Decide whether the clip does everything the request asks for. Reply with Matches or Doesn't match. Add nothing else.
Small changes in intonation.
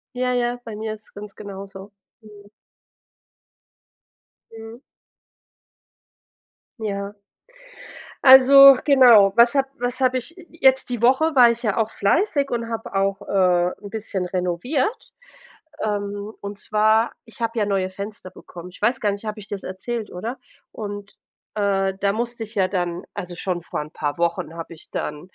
Doesn't match